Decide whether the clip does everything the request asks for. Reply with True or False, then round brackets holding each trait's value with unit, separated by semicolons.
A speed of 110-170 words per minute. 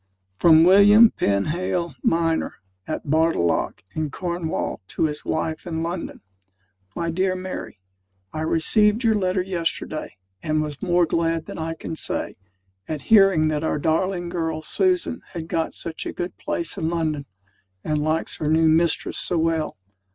True (150 wpm)